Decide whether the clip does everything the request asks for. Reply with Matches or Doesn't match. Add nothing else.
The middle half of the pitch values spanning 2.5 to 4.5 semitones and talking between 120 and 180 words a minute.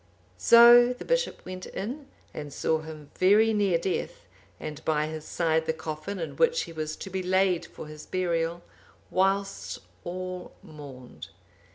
Matches